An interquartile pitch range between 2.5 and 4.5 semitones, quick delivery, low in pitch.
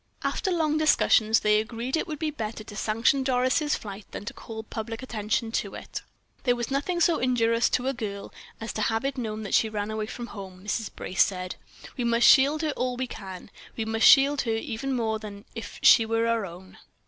No: average, 3.4 semitones; fast, 215 wpm; high, 225 Hz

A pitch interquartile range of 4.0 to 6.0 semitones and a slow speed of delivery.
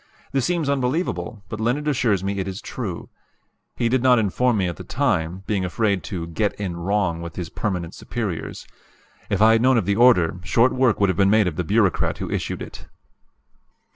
No: average, 4.9 semitones; average, 200 wpm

